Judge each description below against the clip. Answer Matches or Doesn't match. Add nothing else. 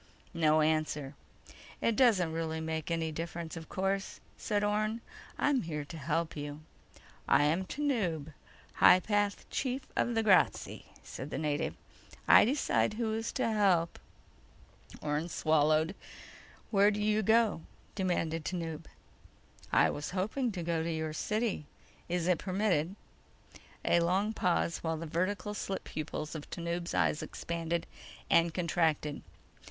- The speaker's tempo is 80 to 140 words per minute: Matches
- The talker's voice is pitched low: Doesn't match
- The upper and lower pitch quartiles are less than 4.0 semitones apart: Doesn't match